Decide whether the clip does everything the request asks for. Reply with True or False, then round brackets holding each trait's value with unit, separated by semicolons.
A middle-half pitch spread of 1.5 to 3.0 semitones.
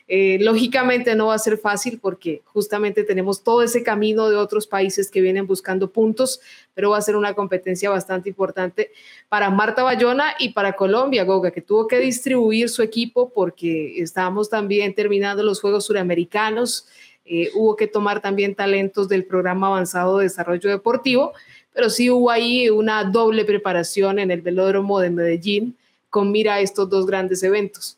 True (2.7 semitones)